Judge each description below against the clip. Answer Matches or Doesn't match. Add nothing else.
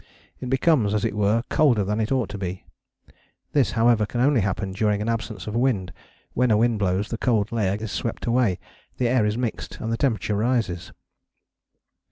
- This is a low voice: Matches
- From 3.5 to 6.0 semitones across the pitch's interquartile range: Doesn't match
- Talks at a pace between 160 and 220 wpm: Matches